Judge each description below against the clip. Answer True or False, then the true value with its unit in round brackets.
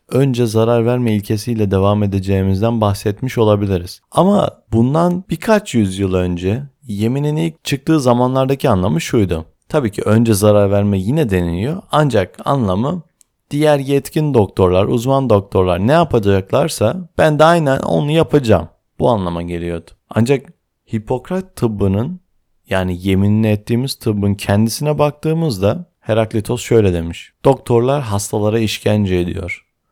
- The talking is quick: False (120 wpm)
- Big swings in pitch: True (6.0 semitones)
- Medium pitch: False (115 Hz)